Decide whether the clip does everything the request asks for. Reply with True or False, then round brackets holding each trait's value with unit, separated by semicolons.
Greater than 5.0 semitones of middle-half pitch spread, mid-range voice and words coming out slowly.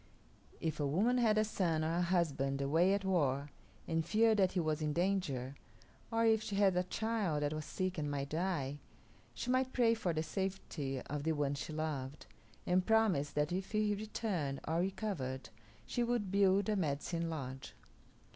False (5.5 semitones; 175 Hz; 185 wpm)